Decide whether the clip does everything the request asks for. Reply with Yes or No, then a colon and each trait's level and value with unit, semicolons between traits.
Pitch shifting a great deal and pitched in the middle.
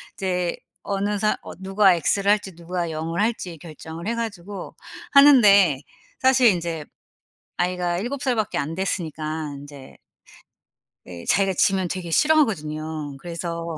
No: average, 4.1 semitones; medium, 180 Hz